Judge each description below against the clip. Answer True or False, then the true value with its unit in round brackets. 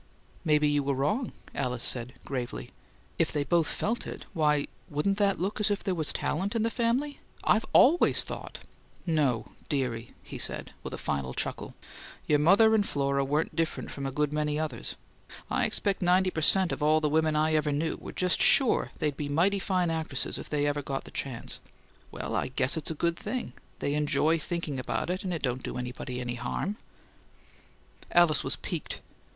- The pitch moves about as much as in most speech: True (4.7 semitones)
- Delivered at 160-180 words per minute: False (195 wpm)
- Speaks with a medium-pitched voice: True (155 Hz)